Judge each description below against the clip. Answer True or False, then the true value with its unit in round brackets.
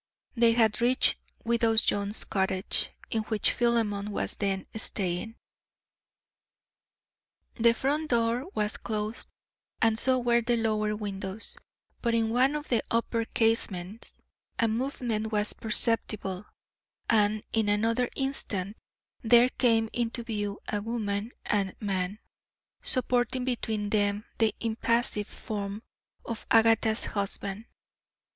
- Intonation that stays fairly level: True (2.2 semitones)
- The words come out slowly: True (115 wpm)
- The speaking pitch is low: False (225 Hz)